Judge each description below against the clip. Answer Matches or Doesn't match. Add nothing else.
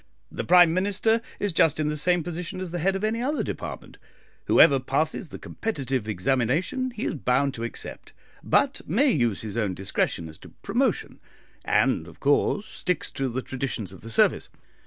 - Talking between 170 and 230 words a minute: Matches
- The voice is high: Doesn't match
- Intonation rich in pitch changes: Matches